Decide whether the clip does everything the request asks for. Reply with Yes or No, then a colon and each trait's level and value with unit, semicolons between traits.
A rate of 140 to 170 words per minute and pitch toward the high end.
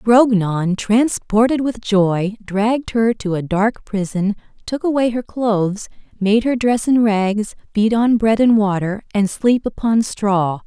Yes: average, 155 wpm; high, 215 Hz